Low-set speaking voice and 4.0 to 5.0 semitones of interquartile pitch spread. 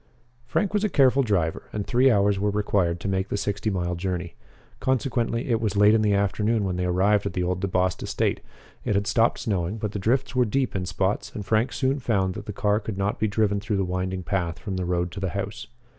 No: low, 100 Hz; average, 3.1 semitones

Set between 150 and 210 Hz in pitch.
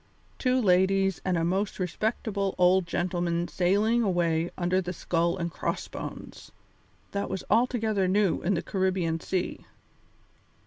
Yes: medium, 185 Hz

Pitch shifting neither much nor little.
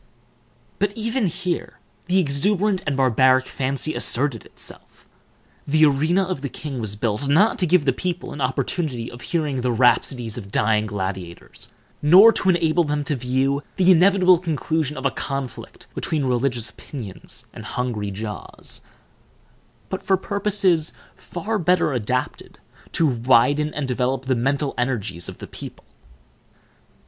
No: wide, 5.8 semitones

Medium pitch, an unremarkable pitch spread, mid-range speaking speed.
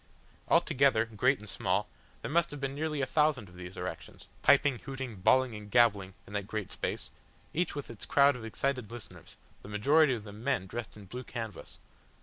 No: low, 120 Hz; average, 4.9 semitones; average, 190 wpm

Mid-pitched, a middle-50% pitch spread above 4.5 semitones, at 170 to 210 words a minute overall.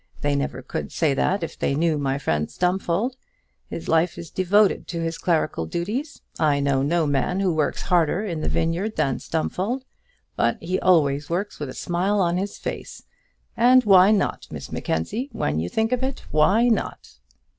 Yes: medium, 170 Hz; wide, 5.4 semitones; average, 180 wpm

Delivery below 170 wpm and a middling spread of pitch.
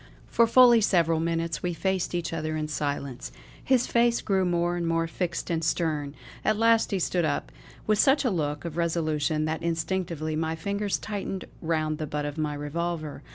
No: average, 185 wpm; average, 3.4 semitones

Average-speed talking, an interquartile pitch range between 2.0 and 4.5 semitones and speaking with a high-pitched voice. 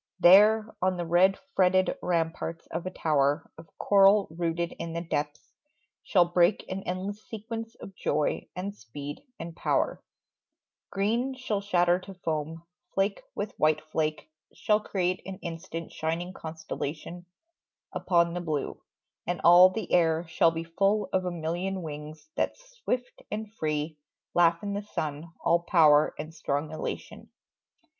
No: average, 145 wpm; average, 3.3 semitones; medium, 175 Hz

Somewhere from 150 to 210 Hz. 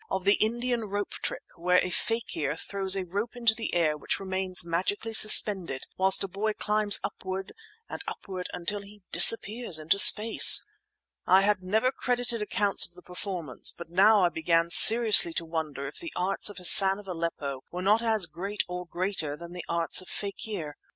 Yes: high, 190 Hz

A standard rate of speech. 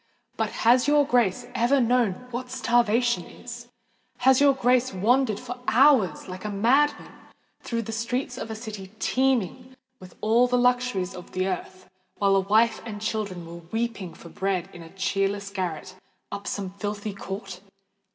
Yes: average, 160 wpm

